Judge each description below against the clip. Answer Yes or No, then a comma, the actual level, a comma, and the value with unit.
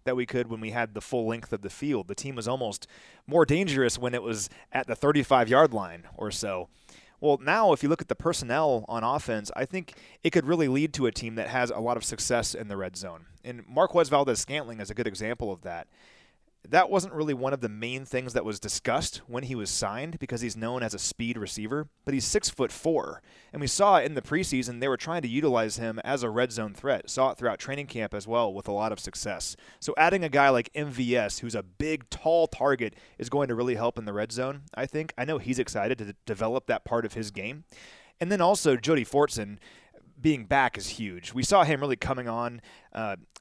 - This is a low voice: Yes, low, 125 Hz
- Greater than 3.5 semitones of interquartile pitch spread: Yes, average, 3.9 semitones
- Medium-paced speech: No, fast, 240 wpm